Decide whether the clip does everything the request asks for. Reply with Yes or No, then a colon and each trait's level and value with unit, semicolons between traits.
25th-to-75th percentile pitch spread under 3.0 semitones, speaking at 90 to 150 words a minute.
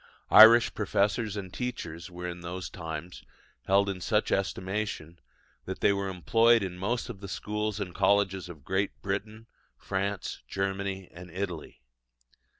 Yes: narrow, 2.5 semitones; average, 145 wpm